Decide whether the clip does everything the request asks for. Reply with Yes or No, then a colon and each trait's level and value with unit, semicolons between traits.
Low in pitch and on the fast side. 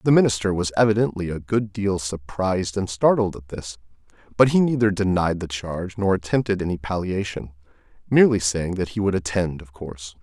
No: very low, 95 Hz; average, 175 wpm